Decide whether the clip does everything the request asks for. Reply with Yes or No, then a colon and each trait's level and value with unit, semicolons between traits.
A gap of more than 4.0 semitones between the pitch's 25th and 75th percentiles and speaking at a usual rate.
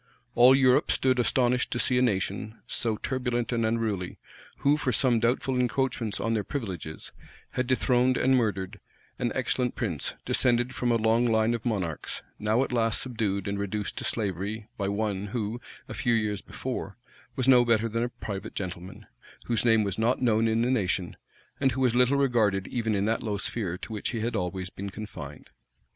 No: average, 3.3 semitones; average, 185 wpm